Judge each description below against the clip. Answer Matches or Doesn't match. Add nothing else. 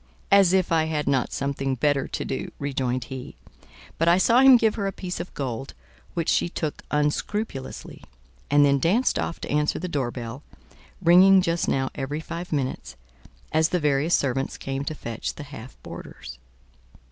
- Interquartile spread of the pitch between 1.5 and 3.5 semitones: Doesn't match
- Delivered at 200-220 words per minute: Doesn't match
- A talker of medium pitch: Matches